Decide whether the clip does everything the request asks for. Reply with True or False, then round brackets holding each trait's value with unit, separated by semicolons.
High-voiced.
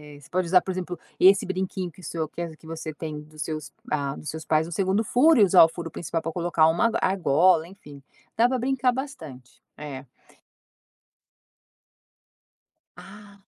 False (170 Hz)